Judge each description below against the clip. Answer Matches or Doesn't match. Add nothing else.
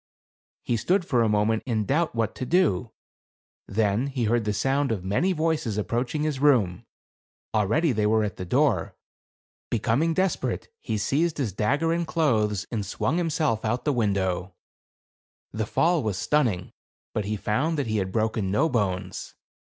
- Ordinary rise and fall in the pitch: Doesn't match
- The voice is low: Matches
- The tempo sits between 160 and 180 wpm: Matches